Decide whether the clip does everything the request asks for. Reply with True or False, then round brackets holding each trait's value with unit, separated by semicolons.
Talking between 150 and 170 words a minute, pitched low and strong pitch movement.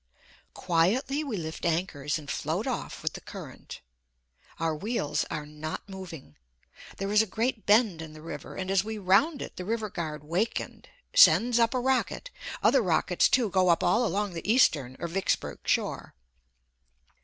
False (165 wpm; 190 Hz; 5.9 semitones)